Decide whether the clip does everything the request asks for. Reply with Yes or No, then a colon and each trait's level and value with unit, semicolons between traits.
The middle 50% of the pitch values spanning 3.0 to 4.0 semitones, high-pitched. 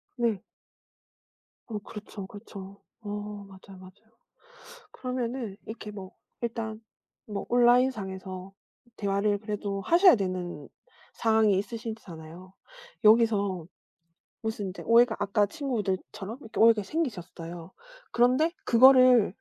Yes: average, 3.3 semitones; high, 210 Hz